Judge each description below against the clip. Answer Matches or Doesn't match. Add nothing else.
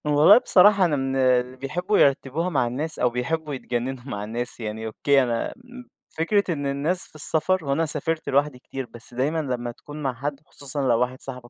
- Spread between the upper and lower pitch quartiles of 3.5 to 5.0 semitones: Matches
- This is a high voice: Doesn't match